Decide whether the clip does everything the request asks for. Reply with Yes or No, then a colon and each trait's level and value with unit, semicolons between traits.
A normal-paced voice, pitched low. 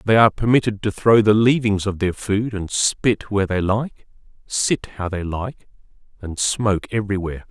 Yes: average, 175 wpm; low, 105 Hz